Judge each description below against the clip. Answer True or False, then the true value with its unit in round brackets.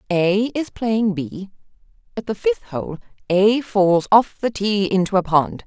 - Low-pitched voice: False (200 Hz)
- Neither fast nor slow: True (170 wpm)